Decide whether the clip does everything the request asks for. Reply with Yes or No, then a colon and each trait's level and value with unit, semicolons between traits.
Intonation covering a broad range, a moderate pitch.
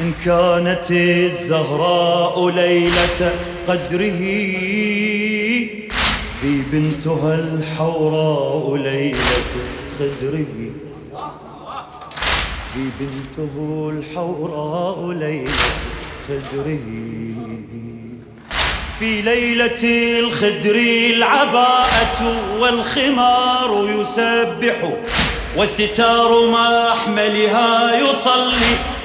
Yes: wide, 7.4 semitones; medium, 175 Hz